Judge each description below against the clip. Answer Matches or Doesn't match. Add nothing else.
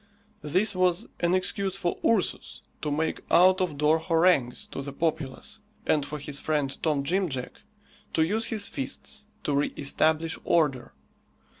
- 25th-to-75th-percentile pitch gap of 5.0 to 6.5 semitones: Doesn't match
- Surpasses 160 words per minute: Doesn't match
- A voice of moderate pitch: Matches